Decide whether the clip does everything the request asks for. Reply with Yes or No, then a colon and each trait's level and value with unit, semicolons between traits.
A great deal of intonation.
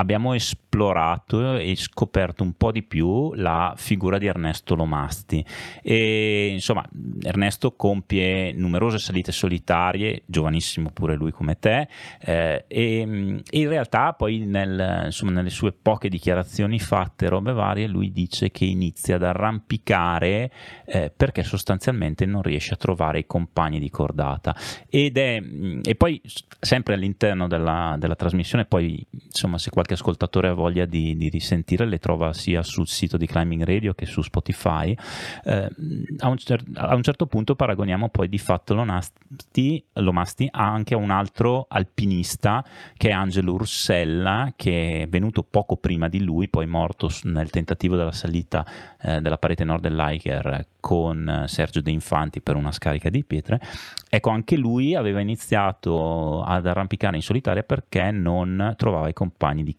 No: average, 4.3 semitones